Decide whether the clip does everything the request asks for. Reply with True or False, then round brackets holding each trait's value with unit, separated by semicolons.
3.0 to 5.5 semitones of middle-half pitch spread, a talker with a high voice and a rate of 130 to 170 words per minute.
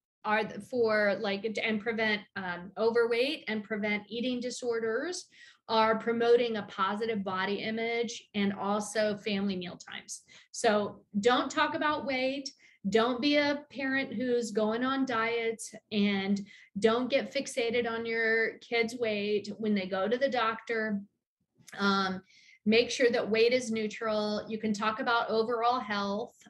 False (2.4 semitones; 225 Hz; 140 wpm)